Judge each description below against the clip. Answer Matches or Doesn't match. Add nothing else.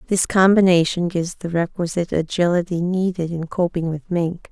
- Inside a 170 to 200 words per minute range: Doesn't match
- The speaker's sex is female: Matches